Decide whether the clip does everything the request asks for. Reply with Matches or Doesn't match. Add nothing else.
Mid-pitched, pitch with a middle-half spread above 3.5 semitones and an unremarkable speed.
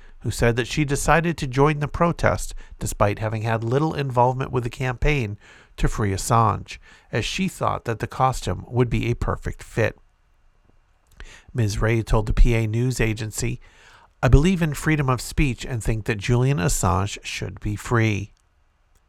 Doesn't match